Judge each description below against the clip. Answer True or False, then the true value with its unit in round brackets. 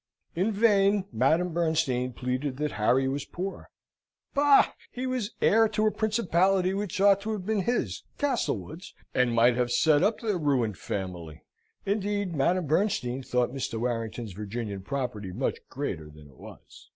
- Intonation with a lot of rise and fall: True (8.8 semitones)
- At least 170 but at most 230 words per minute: False (155 wpm)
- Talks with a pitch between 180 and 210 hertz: False (150 Hz)